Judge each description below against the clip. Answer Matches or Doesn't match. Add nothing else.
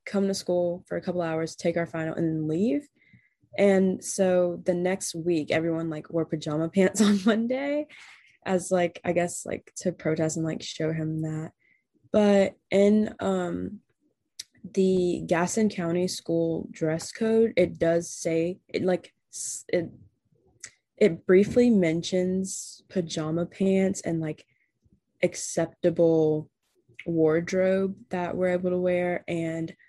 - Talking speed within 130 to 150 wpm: Matches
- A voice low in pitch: Doesn't match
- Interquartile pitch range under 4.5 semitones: Matches